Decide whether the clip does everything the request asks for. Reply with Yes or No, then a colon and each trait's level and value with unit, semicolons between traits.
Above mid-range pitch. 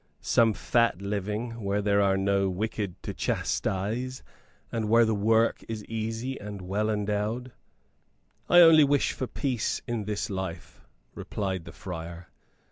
No: low, 105 Hz